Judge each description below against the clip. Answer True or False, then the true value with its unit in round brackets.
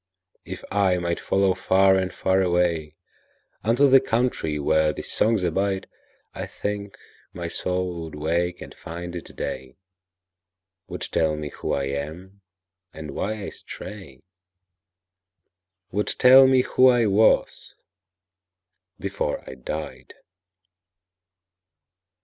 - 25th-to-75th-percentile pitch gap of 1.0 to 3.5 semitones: True (2.6 semitones)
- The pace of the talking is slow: True (110 wpm)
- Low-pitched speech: True (90 Hz)